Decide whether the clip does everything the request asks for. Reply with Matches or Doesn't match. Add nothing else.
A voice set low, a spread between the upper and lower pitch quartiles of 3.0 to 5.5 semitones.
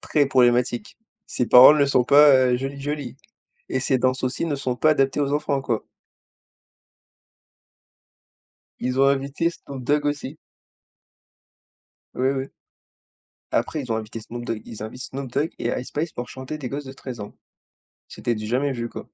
Doesn't match